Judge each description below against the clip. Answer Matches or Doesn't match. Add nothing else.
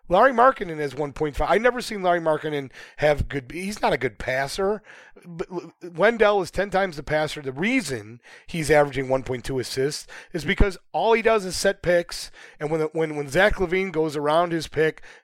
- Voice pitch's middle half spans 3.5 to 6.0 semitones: Matches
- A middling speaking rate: Matches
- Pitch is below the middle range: Doesn't match